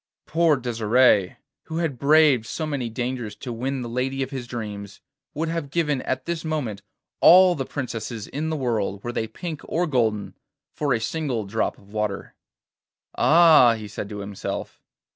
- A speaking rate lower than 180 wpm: Yes, average, 170 wpm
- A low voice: Yes, low, 125 Hz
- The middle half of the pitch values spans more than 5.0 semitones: Yes, wide, 5.5 semitones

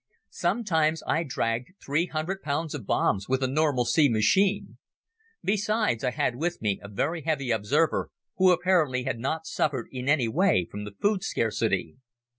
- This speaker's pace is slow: No, average, 165 wpm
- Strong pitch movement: Yes, wide, 6.4 semitones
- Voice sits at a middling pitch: Yes, medium, 145 Hz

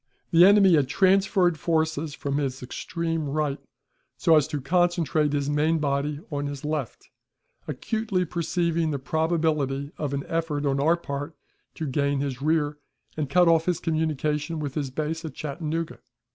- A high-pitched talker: No, medium, 155 Hz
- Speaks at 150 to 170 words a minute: Yes, average, 160 wpm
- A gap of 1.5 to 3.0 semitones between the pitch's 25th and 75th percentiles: Yes, average, 2.7 semitones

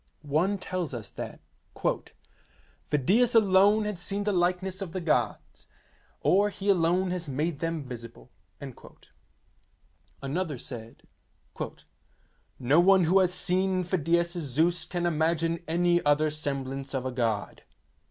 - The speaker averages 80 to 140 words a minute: Yes, slow, 135 wpm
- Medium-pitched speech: Yes, medium, 170 Hz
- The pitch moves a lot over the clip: No, average, 4.3 semitones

